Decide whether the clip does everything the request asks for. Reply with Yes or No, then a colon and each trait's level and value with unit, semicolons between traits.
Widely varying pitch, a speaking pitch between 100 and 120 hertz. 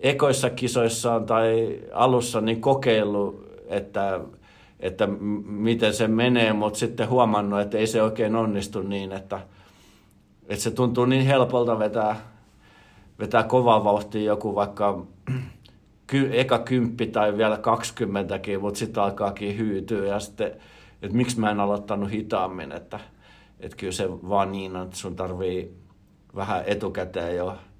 No: narrow, 2.5 semitones; low, 105 Hz